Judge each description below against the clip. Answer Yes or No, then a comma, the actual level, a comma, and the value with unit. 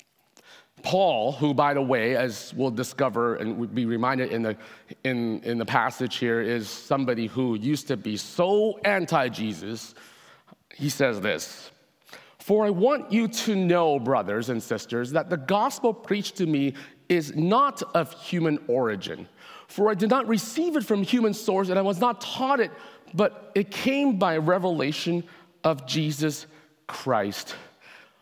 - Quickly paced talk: No, average, 155 wpm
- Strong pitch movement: Yes, wide, 7.8 semitones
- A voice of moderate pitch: Yes, medium, 155 Hz